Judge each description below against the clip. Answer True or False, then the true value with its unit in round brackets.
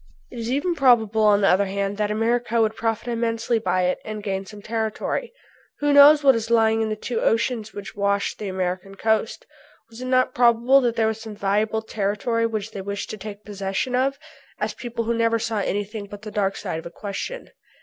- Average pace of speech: False (210 wpm)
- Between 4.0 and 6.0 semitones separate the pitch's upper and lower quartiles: False (2.5 semitones)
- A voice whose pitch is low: False (220 Hz)